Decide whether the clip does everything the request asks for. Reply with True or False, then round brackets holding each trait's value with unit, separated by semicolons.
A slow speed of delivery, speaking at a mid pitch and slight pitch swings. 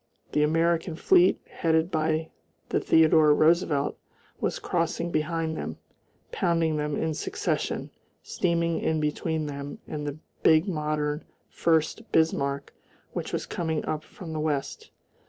True (130 wpm; 160 Hz; 1.7 semitones)